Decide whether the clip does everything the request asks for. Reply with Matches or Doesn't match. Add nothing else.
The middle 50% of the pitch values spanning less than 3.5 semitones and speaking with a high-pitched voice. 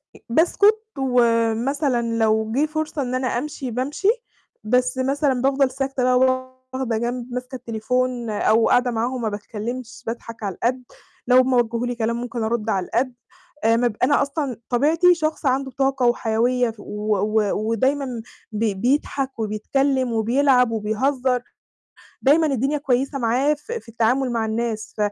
Matches